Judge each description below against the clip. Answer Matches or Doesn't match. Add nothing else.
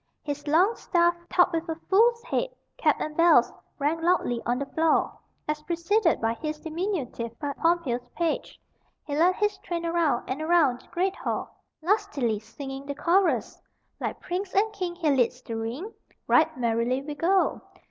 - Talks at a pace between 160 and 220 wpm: Matches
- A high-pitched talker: Matches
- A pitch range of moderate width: Matches